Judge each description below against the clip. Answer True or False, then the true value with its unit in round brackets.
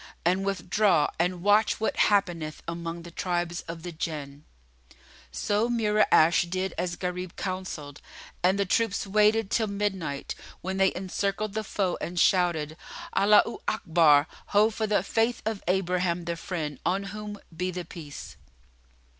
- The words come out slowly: False (145 wpm)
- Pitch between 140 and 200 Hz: True (185 Hz)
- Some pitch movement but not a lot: True (3.3 semitones)